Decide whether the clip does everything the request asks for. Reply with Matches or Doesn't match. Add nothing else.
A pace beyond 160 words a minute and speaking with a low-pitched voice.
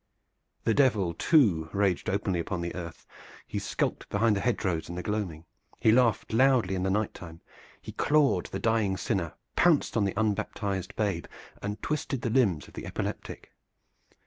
Matches